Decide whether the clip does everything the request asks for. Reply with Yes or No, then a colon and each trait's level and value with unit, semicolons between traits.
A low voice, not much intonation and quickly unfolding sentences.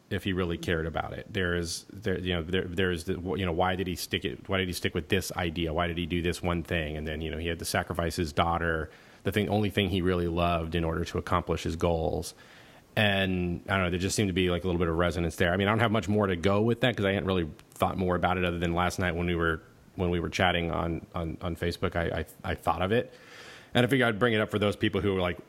Yes: very low, 90 Hz; narrow, 2.3 semitones; fast, 300 wpm